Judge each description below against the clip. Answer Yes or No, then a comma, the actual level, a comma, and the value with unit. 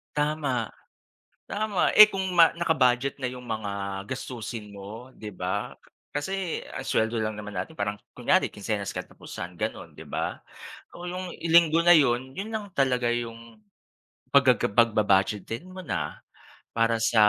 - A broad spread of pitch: Yes, wide, 7.1 semitones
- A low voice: Yes, low, 120 Hz